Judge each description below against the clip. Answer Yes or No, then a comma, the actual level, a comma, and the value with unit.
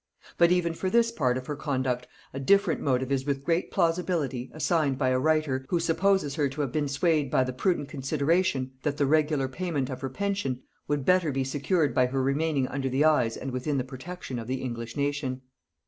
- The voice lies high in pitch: No, medium, 140 Hz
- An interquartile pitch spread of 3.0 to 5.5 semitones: Yes, average, 3.8 semitones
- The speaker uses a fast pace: Yes, fast, 210 wpm